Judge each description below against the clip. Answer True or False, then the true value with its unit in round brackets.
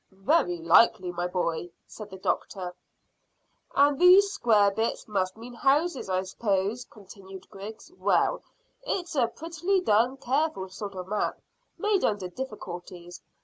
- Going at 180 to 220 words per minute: False (135 wpm)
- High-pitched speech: True (215 Hz)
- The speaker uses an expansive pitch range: True (6.8 semitones)